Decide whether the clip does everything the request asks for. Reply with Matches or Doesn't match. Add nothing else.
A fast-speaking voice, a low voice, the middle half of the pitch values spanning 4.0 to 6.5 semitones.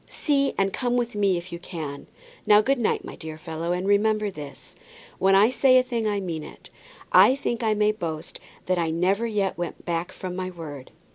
Doesn't match